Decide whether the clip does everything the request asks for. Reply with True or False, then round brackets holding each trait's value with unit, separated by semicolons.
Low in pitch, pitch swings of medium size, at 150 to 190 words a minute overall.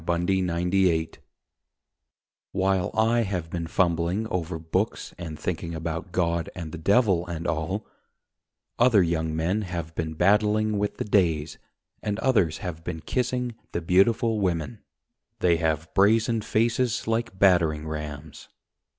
False (90 Hz; 4.3 semitones; 135 wpm)